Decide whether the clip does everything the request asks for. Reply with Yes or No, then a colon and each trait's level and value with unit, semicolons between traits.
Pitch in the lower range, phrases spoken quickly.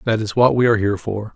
Yes: low, 110 Hz; fast, 310 wpm